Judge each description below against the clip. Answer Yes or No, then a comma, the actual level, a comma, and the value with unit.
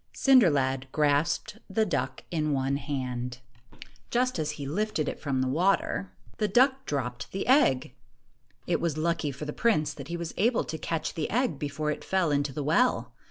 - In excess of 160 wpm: Yes, average, 195 wpm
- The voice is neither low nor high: Yes, medium, 155 Hz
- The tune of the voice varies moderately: No, wide, 5.9 semitones